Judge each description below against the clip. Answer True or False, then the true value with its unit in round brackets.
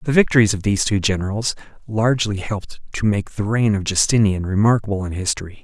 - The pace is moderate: True (180 wpm)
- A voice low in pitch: True (105 Hz)